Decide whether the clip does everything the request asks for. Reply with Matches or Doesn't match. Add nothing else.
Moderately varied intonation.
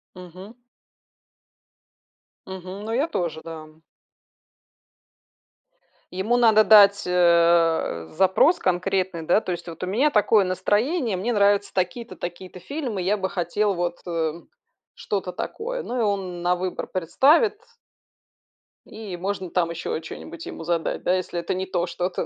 Matches